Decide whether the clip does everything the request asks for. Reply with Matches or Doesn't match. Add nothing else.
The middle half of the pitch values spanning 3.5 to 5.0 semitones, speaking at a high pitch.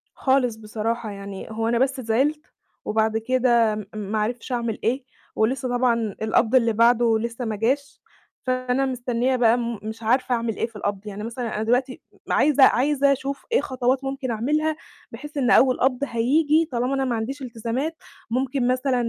Doesn't match